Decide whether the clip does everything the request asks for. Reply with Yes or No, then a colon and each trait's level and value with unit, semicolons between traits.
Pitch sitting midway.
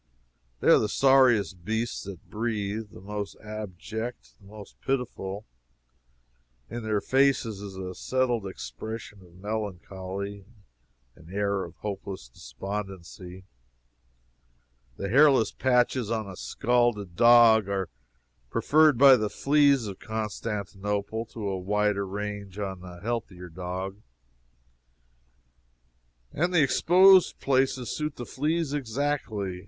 No: low, 105 Hz